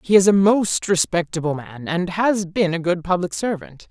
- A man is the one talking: No, female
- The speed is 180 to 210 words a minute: Yes, average, 200 wpm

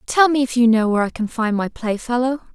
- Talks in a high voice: Yes, high, 240 Hz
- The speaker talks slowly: No, fast, 260 wpm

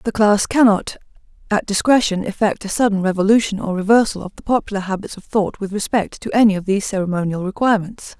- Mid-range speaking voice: No, high, 205 Hz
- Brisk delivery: No, average, 185 wpm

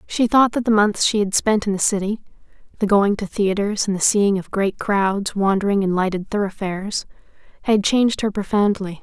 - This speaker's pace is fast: No, average, 195 wpm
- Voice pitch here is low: No, high, 205 Hz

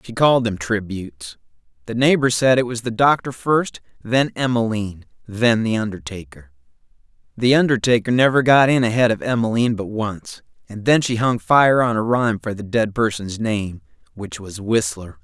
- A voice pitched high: No, low, 115 Hz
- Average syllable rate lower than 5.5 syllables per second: Yes, 5.1 syllables/s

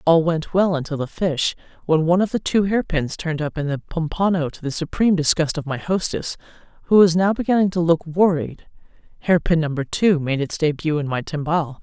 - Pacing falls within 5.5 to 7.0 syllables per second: Yes, 5.7 syllables/s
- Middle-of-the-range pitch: Yes, medium, 165 Hz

